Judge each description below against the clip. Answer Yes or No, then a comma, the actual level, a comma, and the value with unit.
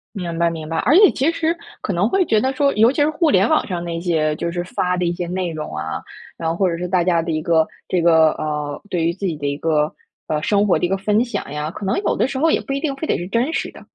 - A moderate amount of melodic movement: No, wide, 5.7 semitones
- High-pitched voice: No, medium, 175 Hz